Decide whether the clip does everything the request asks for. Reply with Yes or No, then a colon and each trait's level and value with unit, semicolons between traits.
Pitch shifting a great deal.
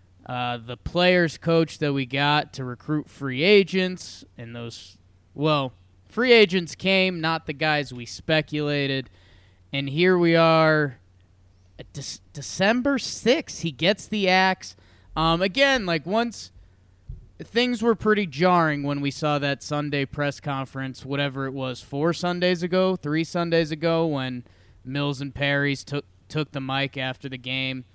No: average, 4.8 semitones